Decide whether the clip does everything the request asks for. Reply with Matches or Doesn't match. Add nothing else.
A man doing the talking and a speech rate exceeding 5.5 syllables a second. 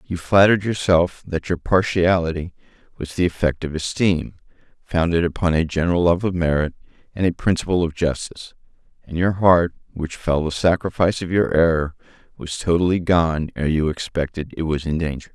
Doesn't match